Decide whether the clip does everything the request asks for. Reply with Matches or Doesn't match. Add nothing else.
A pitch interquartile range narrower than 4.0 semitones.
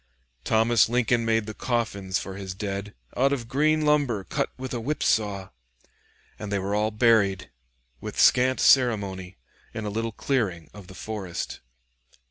Matches